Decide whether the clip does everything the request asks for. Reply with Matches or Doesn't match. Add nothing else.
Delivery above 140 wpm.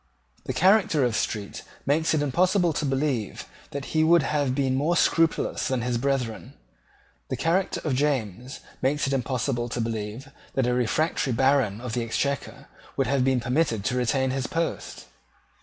Matches